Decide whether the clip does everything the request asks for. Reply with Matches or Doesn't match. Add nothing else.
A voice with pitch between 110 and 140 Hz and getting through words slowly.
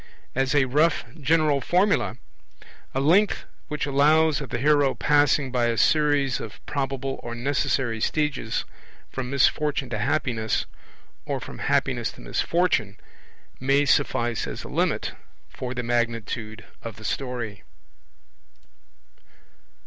Matches